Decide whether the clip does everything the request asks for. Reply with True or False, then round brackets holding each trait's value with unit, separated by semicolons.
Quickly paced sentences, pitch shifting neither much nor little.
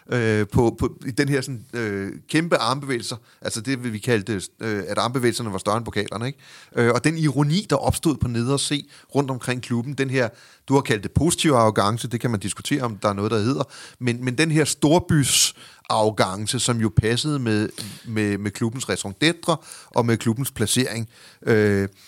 False (180 wpm; 4.1 semitones)